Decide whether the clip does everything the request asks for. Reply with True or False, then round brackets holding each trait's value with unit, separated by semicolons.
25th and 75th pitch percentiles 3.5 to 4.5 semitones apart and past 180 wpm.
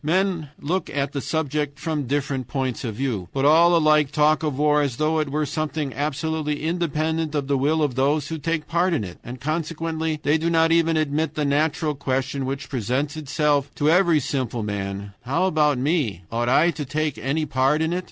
False (2.8 semitones; 200 wpm)